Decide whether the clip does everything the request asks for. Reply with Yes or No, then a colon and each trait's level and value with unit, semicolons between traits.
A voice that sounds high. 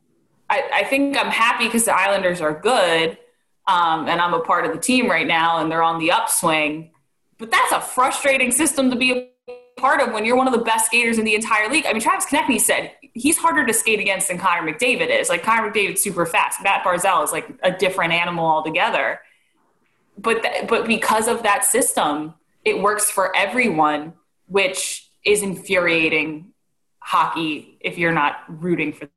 Yes: high, 200 Hz